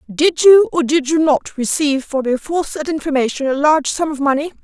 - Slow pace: No, fast, 205 wpm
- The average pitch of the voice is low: No, very high, 295 Hz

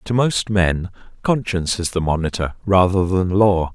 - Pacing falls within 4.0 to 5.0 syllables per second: Yes, 4.6 syllables/s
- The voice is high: No, very low, 95 Hz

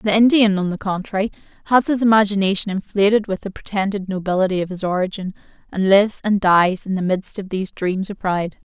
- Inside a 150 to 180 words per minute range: No, average, 195 wpm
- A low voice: No, high, 195 Hz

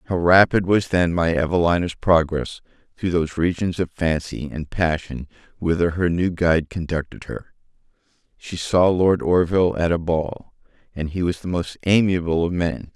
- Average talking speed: Yes, average, 155 wpm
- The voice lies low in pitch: Yes, very low, 85 Hz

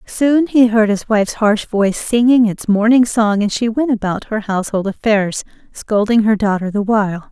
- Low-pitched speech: No, high, 215 Hz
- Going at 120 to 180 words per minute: No, average, 190 wpm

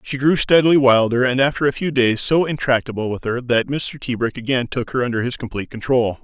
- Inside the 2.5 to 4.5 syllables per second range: No, 5.9 syllables/s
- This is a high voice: No, low, 125 Hz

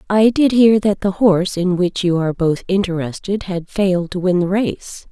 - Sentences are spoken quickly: Yes, fast, 210 wpm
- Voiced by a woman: Yes, female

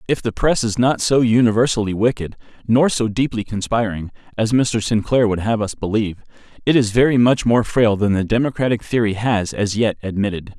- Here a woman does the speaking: No, male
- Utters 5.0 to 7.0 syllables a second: Yes, 5.5 syllables/s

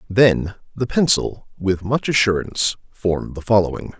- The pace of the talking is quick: No, slow, 135 wpm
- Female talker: No, male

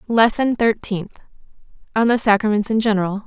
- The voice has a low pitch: No, high, 215 Hz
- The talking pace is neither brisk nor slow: No, slow, 130 wpm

